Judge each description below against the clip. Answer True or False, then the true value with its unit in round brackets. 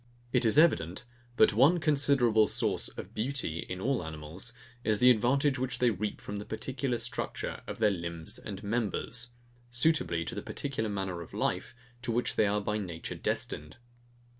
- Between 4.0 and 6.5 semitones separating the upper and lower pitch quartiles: True (4.8 semitones)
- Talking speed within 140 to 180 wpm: True (170 wpm)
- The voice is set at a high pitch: False (110 Hz)